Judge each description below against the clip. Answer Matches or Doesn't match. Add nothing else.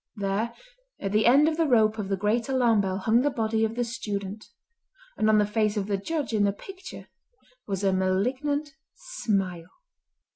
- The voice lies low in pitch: Doesn't match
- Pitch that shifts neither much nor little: Matches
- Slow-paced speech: Doesn't match